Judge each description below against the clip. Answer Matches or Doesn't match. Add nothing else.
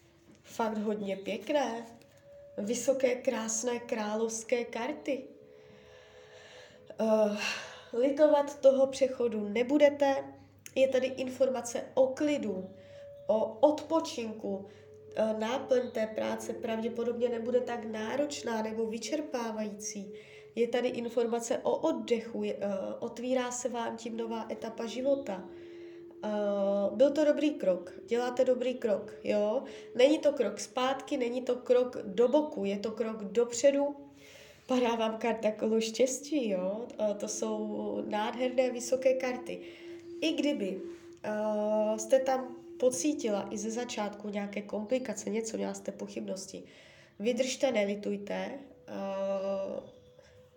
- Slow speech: Matches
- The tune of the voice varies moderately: Matches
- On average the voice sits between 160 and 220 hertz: Doesn't match